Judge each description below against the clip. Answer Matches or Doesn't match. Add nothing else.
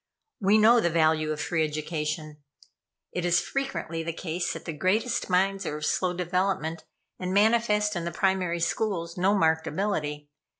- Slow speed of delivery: Doesn't match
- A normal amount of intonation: Matches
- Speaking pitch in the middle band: Matches